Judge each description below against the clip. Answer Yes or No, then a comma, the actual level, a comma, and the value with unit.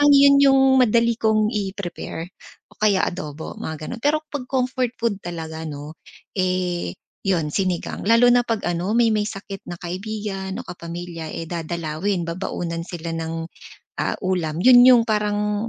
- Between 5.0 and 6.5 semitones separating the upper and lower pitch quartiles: Yes, average, 5.3 semitones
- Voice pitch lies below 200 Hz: Yes, high, 190 Hz